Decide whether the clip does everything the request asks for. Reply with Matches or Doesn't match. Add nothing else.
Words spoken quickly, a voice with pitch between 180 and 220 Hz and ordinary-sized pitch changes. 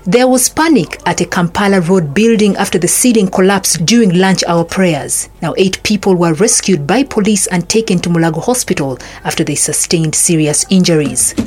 Doesn't match